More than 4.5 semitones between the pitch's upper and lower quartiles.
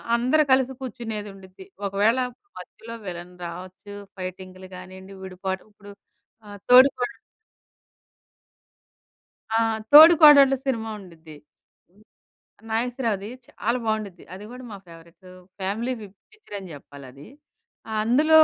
Yes: average, 5.0 semitones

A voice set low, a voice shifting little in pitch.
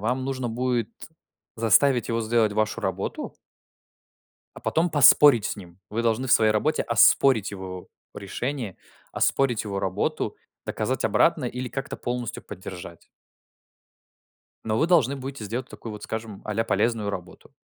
No: low, 115 Hz; average, 3.5 semitones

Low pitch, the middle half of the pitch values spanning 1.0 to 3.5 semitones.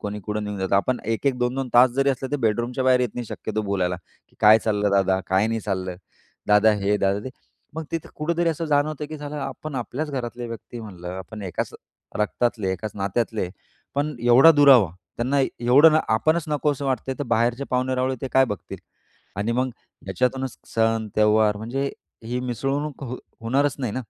No: low, 120 Hz; average, 4.3 semitones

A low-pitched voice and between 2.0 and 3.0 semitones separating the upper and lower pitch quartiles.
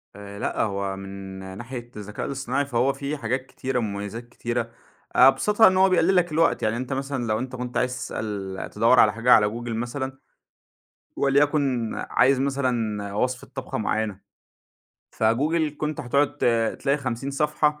No: low, 125 Hz; average, 4.1 semitones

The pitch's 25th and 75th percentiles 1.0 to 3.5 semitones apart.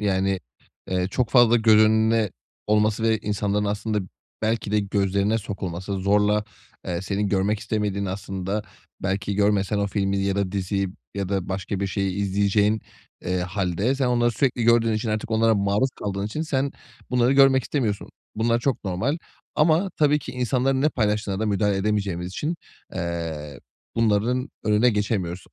Yes: average, 2.7 semitones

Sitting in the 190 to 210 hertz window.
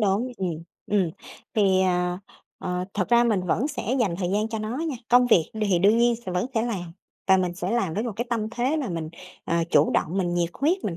Yes: high, 200 Hz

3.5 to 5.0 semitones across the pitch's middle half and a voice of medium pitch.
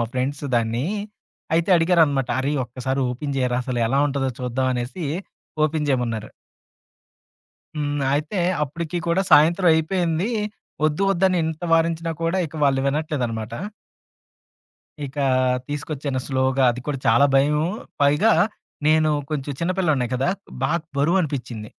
Yes: average, 3.8 semitones; medium, 145 Hz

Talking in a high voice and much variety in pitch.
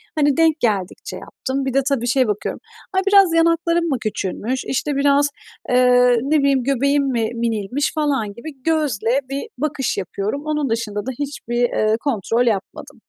No: very high, 265 Hz; average, 3.9 semitones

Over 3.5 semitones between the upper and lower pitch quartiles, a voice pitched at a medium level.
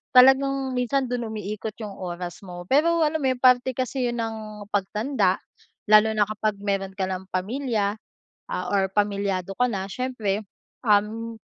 No: average, 4.2 semitones; high, 215 Hz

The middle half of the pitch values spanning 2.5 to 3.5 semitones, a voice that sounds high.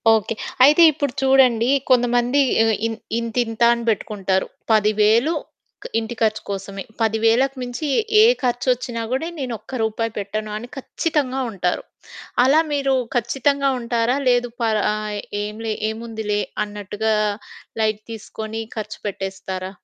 Yes: average, 2.9 semitones; high, 225 Hz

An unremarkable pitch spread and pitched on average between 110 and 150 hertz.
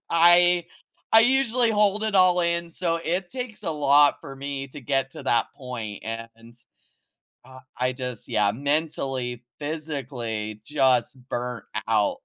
No: wide, 6.0 semitones; medium, 140 Hz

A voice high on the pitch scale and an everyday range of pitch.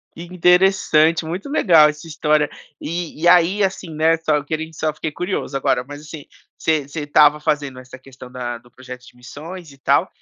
No: medium, 155 Hz; average, 3.1 semitones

